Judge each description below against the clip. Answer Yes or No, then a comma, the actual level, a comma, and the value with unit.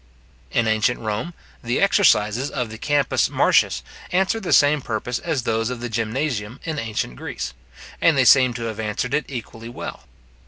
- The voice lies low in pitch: Yes, low, 120 Hz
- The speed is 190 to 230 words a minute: No, average, 170 wpm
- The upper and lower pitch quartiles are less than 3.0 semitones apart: No, average, 4.6 semitones